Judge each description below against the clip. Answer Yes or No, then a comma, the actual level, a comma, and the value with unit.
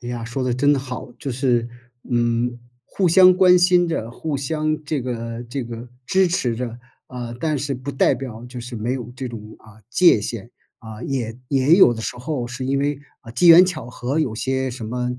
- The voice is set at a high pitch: No, low, 125 Hz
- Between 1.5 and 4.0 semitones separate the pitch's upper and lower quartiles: Yes, average, 3.5 semitones